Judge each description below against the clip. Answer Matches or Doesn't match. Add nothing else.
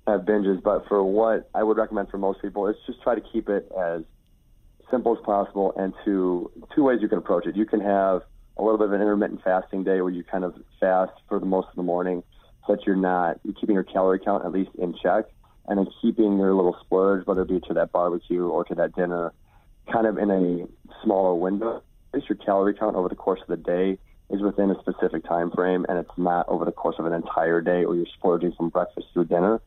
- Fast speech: Matches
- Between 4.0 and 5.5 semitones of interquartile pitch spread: Doesn't match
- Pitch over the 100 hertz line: Doesn't match